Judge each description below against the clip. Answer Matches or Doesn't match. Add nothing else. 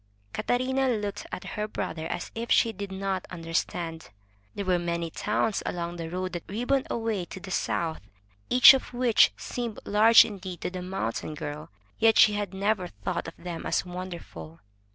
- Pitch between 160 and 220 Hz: Matches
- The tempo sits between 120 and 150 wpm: Doesn't match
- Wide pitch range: Doesn't match